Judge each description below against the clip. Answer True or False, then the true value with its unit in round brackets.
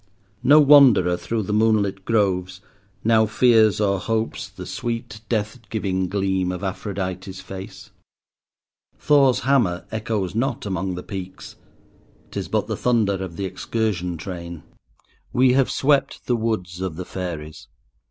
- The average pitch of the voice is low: True (100 Hz)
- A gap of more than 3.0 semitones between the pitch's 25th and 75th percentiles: True (3.5 semitones)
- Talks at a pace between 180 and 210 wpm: False (135 wpm)